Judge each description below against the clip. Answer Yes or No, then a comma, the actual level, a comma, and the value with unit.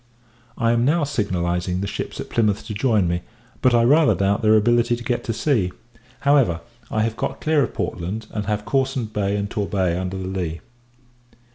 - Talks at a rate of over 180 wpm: Yes, average, 190 wpm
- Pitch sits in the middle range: No, low, 105 Hz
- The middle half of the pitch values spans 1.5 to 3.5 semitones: No, average, 4.0 semitones